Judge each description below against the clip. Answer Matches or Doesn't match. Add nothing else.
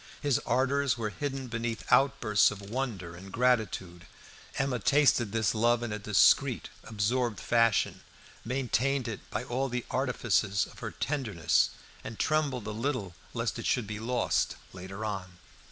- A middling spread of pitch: Matches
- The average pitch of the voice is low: Matches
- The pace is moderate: Matches